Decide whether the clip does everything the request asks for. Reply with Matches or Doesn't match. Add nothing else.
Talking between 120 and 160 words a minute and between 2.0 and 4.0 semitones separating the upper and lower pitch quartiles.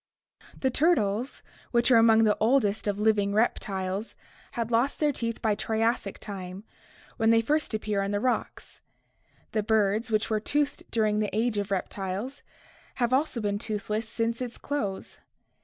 Matches